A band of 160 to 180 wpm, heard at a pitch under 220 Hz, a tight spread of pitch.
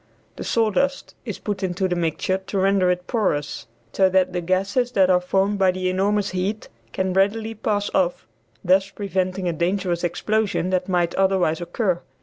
Yes: average, 170 wpm; high, 190 Hz; narrow, 2.0 semitones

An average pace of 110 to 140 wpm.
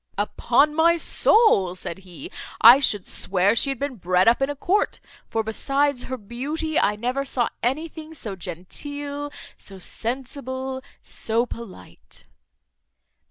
Yes: slow, 135 wpm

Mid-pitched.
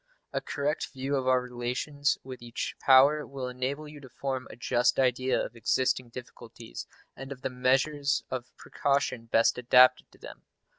No: low, 130 Hz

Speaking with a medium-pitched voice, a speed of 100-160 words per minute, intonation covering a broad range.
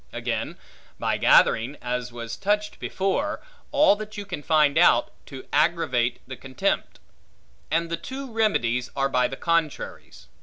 Yes: medium, 155 Hz; average, 145 wpm; wide, 8.2 semitones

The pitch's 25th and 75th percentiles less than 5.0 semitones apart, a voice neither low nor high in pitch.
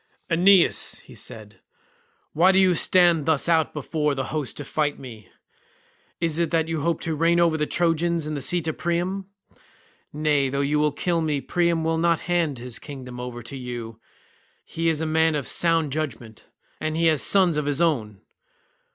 Yes: average, 3.3 semitones; medium, 155 Hz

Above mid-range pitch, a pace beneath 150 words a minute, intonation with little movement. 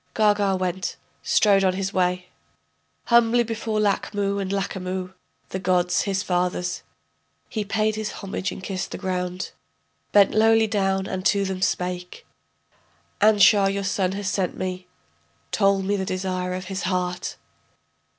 Yes: high, 195 Hz; average, 140 wpm; narrow, 1.8 semitones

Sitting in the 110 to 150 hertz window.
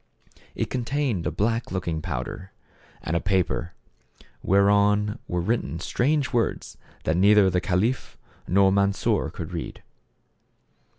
No: low, 100 Hz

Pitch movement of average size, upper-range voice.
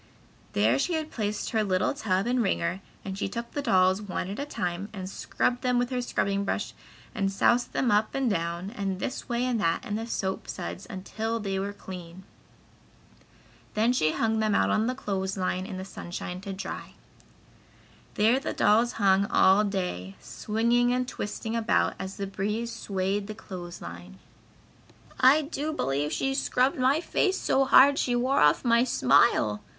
Yes: average, 4.4 semitones; high, 205 Hz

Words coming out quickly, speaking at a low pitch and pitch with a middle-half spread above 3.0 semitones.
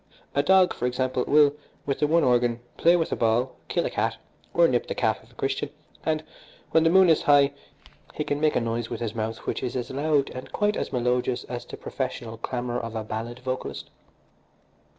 Yes: fast, 210 wpm; low, 130 Hz; average, 4.1 semitones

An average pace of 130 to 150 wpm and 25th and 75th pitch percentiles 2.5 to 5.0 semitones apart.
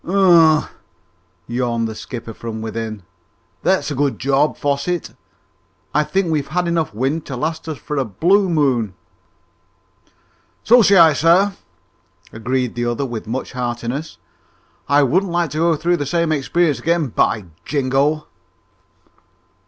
No: average, 140 wpm; wide, 5.5 semitones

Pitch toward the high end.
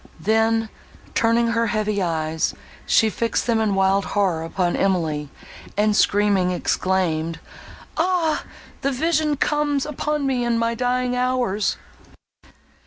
Yes: high, 225 Hz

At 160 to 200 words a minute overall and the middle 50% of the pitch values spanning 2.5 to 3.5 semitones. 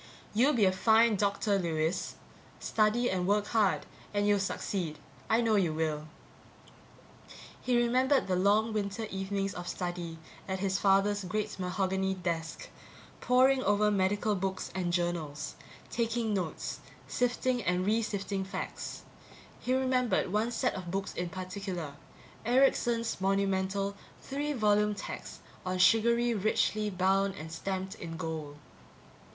No: slow, 135 wpm; average, 3.1 semitones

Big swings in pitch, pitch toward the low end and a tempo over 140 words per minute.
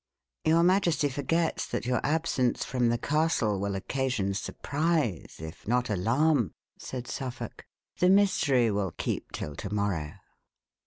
No: wide, 7.5 semitones; low, 125 Hz; slow, 135 wpm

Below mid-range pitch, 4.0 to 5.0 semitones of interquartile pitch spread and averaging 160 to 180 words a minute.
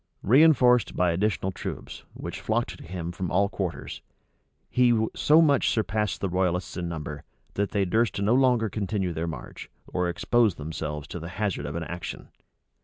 Yes: very low, 95 Hz; average, 4.4 semitones; average, 170 wpm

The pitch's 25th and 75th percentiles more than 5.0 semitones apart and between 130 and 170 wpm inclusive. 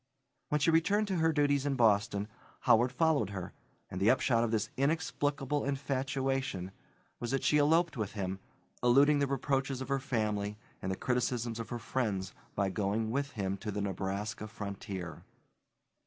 Yes: wide, 5.4 semitones; average, 165 wpm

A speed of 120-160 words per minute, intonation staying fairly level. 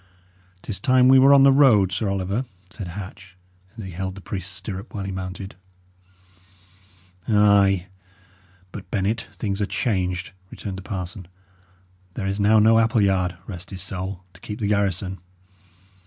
Yes: average, 155 wpm; narrow, 2.2 semitones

